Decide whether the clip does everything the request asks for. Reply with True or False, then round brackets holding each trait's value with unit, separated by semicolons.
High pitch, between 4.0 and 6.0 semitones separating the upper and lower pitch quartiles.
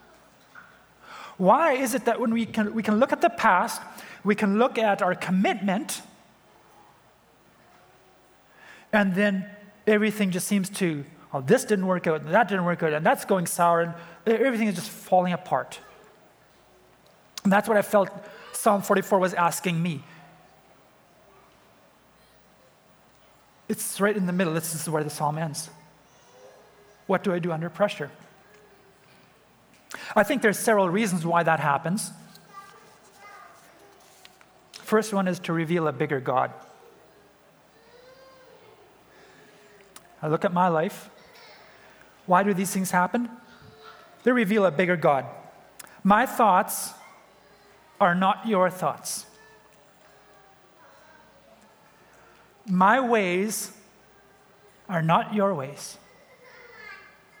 False (200 Hz; 3.5 semitones)